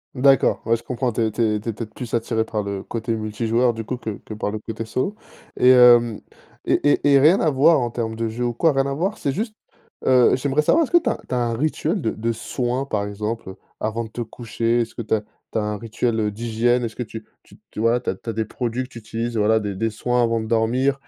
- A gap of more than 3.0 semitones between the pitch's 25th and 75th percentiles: No, narrow, 2.4 semitones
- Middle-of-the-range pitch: No, low, 115 Hz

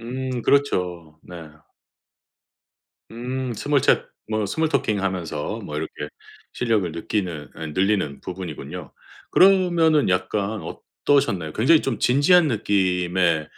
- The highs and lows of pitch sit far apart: Yes, wide, 6.8 semitones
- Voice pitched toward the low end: Yes, low, 105 Hz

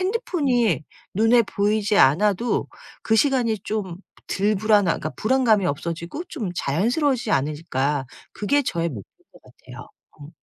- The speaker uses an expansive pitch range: Yes, wide, 6.2 semitones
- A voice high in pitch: Yes, high, 210 Hz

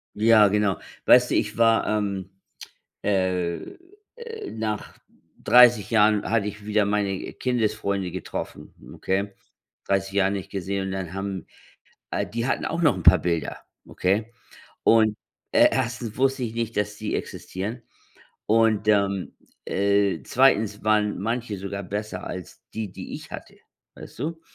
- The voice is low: Yes, low, 105 Hz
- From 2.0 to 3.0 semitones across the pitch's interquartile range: Yes, narrow, 2.6 semitones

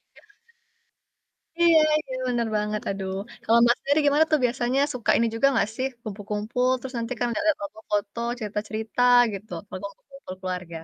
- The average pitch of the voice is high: Yes, high, 230 Hz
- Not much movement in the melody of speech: No, average, 3.7 semitones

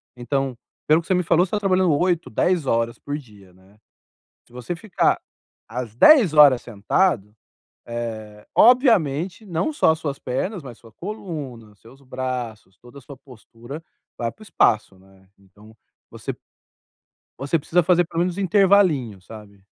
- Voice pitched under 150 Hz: Yes, low, 135 Hz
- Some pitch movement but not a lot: No, wide, 7.6 semitones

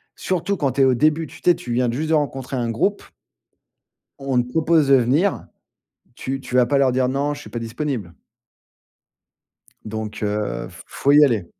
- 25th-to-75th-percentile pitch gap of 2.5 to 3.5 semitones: No, average, 4.0 semitones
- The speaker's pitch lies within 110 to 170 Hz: Yes, low, 135 Hz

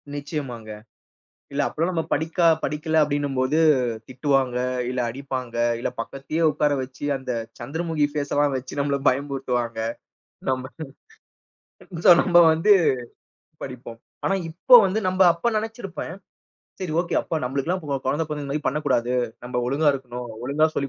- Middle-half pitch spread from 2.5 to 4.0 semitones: Yes, average, 3.6 semitones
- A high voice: No, medium, 145 Hz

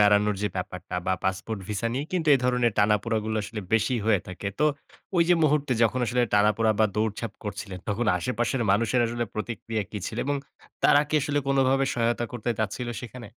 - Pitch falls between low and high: No, low, 115 Hz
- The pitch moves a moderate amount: Yes, average, 3.3 semitones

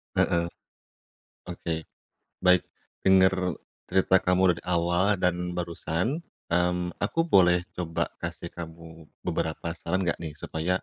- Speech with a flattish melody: Yes, narrow, 1.6 semitones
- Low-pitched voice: Yes, very low, 90 Hz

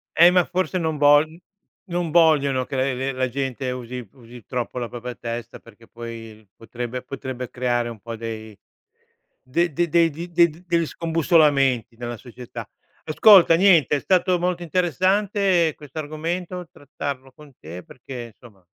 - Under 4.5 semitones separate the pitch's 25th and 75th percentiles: No, wide, 5.7 semitones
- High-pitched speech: No, medium, 140 Hz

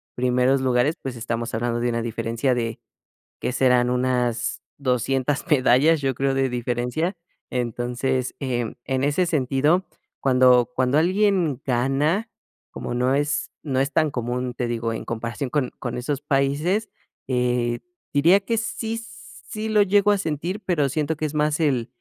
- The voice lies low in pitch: Yes, low, 130 Hz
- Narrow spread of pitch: No, average, 3.8 semitones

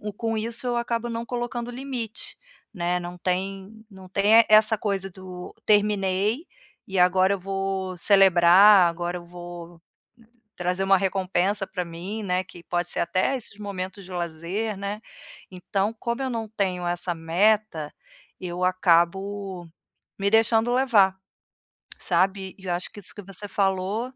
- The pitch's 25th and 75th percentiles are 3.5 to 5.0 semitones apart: No, average, 3.1 semitones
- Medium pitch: No, high, 195 Hz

